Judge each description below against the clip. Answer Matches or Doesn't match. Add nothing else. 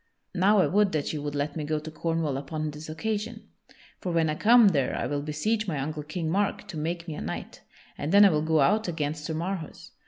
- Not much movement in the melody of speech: Doesn't match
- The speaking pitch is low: Doesn't match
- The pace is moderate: Doesn't match